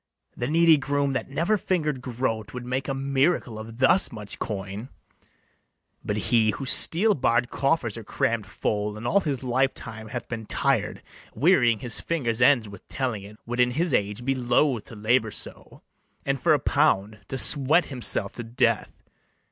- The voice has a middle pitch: No, low, 125 Hz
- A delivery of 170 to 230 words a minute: Yes, average, 175 wpm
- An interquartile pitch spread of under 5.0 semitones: Yes, average, 3.8 semitones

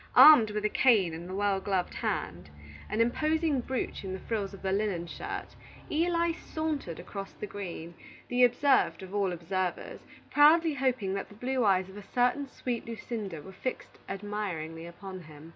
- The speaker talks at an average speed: Yes, average, 175 wpm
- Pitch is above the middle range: Yes, high, 205 Hz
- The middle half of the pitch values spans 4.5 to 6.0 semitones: Yes, average, 5.1 semitones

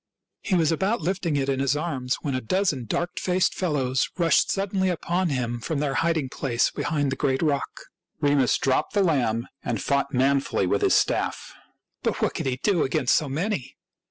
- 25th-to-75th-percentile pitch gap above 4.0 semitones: Yes, average, 4.7 semitones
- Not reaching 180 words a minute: No, average, 185 wpm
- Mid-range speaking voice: Yes, medium, 145 Hz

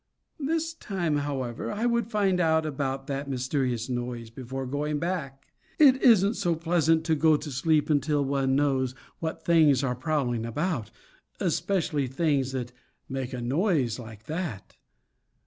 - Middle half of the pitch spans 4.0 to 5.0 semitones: Yes, average, 4.4 semitones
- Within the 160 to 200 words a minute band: No, average, 145 wpm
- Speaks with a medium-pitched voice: Yes, medium, 145 Hz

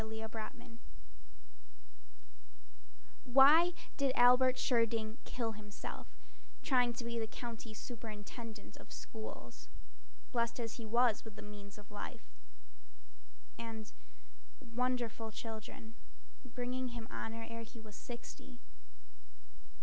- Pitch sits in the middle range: No, high, 230 Hz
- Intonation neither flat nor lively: No, narrow, 2.1 semitones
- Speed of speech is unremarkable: No, slow, 105 wpm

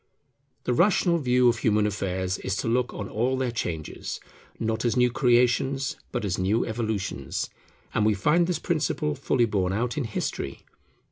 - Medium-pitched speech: No, low, 115 Hz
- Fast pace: No, average, 165 wpm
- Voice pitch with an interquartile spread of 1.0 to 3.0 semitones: No, average, 3.5 semitones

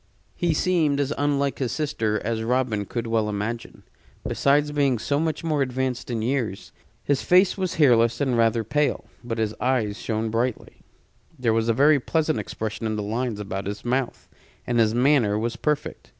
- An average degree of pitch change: Yes, average, 4.2 semitones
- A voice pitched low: Yes, low, 125 Hz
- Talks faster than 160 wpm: Yes, average, 180 wpm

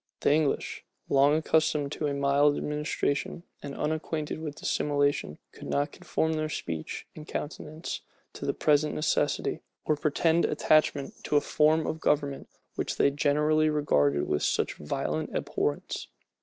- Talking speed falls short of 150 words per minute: Yes, average, 140 wpm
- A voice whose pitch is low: No, medium, 150 Hz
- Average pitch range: No, narrow, 1.5 semitones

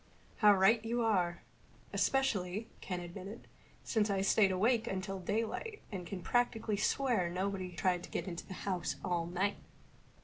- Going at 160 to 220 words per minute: No, average, 150 wpm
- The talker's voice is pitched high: Yes, high, 195 Hz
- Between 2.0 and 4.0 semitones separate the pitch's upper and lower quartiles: Yes, average, 3.4 semitones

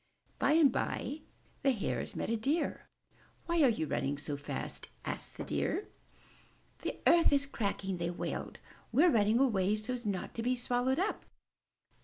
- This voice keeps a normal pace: Yes, average, 165 wpm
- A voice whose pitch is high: Yes, high, 240 Hz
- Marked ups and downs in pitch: Yes, wide, 5.7 semitones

